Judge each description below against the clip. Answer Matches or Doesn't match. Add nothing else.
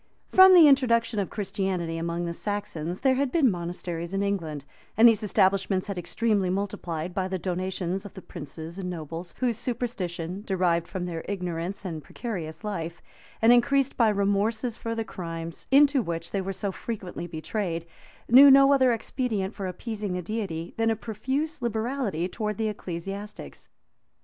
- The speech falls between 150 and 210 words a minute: Matches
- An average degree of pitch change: Matches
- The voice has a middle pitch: Doesn't match